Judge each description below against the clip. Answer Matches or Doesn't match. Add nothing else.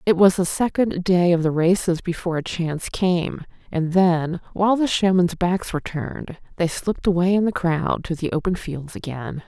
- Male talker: Doesn't match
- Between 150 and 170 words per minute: Doesn't match